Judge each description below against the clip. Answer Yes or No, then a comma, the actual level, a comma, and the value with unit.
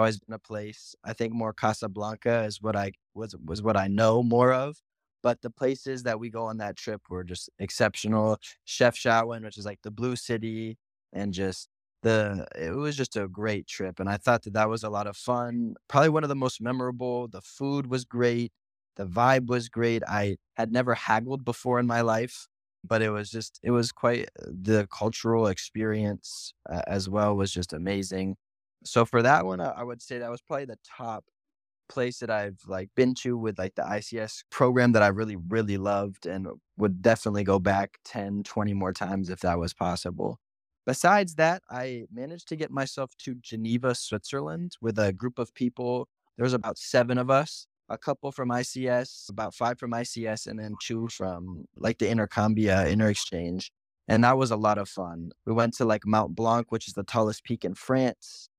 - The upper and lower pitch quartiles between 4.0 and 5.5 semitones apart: No, average, 3.2 semitones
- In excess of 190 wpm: Yes, average, 200 wpm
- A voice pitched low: Yes, low, 110 Hz